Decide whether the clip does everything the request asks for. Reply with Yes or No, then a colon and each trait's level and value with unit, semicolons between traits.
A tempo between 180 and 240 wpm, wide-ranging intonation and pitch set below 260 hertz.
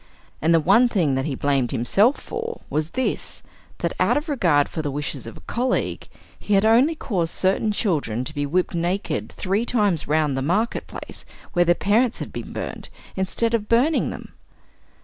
Yes: average, 190 wpm; wide, 7.7 semitones; medium, 185 Hz